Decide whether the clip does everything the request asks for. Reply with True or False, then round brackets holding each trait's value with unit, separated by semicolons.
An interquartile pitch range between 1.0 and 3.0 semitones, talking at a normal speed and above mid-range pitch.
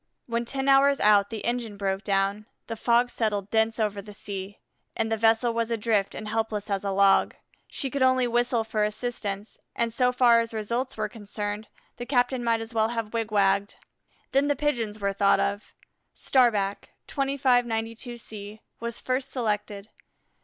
True (2.7 semitones; 165 wpm; 225 Hz)